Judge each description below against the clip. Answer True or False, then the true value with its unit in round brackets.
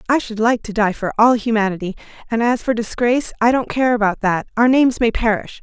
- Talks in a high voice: True (230 Hz)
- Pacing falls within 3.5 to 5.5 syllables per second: False (6.0 syllables/s)